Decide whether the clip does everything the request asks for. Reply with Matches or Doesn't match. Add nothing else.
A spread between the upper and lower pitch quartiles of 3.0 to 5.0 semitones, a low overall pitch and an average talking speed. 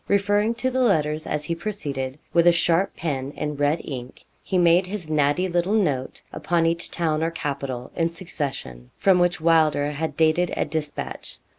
Doesn't match